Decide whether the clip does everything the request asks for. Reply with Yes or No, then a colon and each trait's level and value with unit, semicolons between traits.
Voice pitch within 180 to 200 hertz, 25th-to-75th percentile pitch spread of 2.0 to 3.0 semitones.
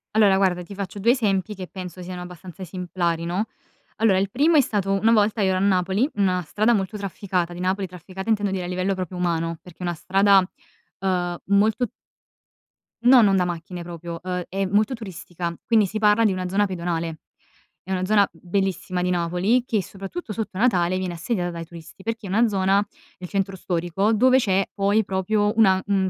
Yes: high, 190 Hz; narrow, 2.5 semitones